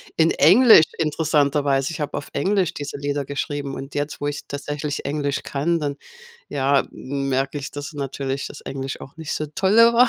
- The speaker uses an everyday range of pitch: No, narrow, 2.2 semitones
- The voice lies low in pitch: No, medium, 145 Hz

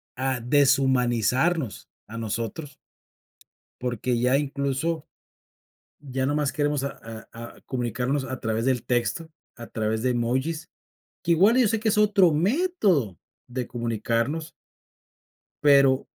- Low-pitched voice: Yes, low, 130 Hz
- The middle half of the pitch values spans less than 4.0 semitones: No, average, 4.7 semitones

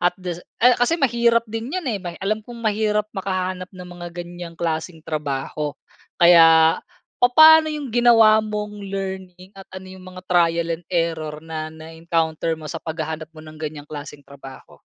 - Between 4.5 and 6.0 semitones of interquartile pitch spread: Yes, average, 4.8 semitones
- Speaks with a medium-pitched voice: Yes, medium, 180 Hz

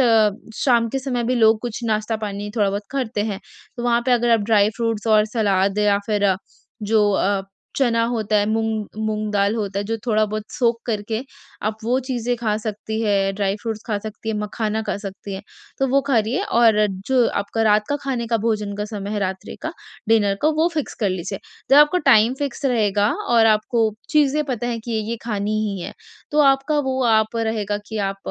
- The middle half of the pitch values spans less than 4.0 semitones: Yes, narrow, 2.5 semitones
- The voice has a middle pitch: No, high, 220 Hz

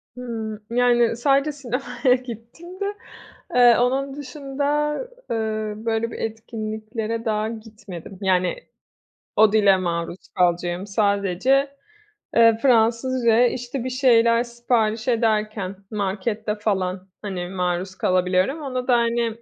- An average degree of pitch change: Yes, average, 3.4 semitones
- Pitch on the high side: Yes, high, 225 Hz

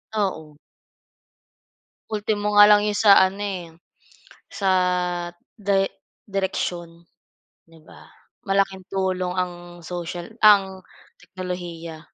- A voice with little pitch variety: Yes, narrow, 2.3 semitones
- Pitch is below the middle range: No, high, 190 Hz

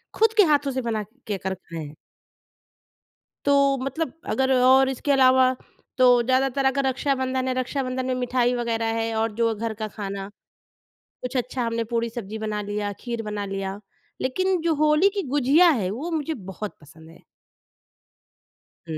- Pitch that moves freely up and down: No, average, 4.1 semitones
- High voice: Yes, very high, 255 Hz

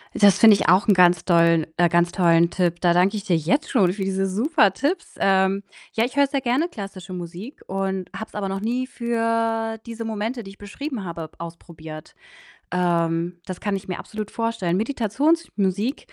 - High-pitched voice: Yes, high, 195 Hz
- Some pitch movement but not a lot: Yes, average, 4.4 semitones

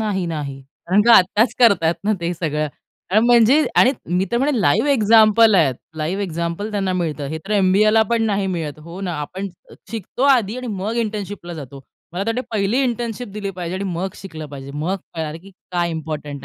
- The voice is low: No, high, 195 Hz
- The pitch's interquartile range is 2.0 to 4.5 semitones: No, average, 4.9 semitones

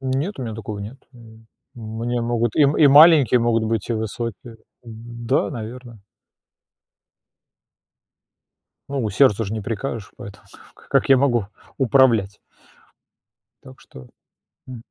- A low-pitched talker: Yes, low, 115 Hz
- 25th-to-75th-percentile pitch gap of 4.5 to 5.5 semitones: No, average, 2.9 semitones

